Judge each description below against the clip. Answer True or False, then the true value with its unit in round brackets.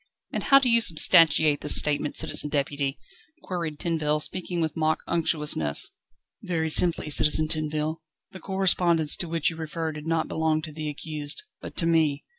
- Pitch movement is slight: True (1.9 semitones)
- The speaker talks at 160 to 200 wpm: True (165 wpm)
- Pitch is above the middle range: False (160 Hz)